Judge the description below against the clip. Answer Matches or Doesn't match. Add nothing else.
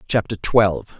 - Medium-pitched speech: Doesn't match